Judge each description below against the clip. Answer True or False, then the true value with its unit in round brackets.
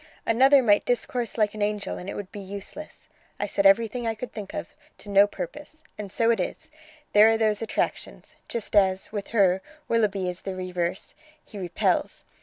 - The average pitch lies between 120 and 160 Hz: False (205 Hz)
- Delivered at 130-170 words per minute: False (190 wpm)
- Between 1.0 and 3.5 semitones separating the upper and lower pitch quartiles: True (2.8 semitones)